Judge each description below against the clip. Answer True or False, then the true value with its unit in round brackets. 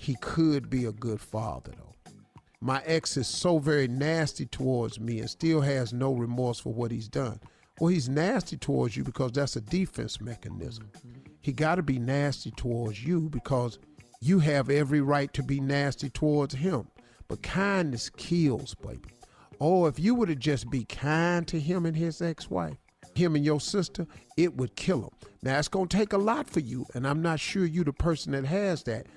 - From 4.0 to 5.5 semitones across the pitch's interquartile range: True (5.0 semitones)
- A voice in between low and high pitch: True (145 Hz)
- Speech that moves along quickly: False (195 wpm)